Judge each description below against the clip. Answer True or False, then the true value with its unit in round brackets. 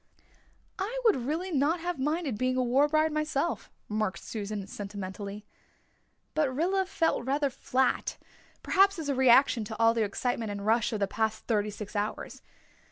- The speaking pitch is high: True (255 Hz)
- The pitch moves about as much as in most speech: False (6.3 semitones)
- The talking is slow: False (165 wpm)